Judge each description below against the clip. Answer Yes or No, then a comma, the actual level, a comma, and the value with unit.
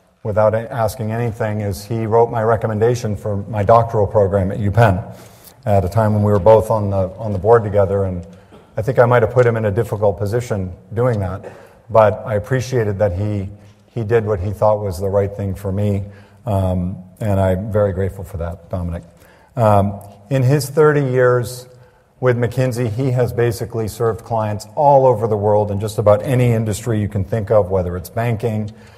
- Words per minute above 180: Yes, average, 195 wpm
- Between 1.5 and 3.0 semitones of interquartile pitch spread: Yes, narrow, 2.6 semitones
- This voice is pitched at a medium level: No, low, 110 Hz